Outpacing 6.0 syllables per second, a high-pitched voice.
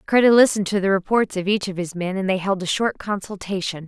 Yes: 6.2 syllables/s; high, 195 Hz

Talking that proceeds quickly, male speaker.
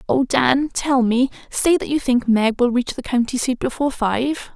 No: fast, 210 wpm; female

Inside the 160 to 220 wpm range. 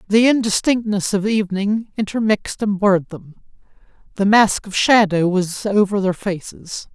No: average, 140 wpm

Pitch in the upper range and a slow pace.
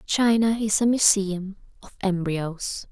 Yes: high, 200 Hz; slow, 125 wpm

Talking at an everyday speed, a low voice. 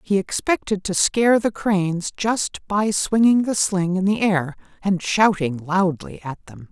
No: average, 170 wpm; high, 190 Hz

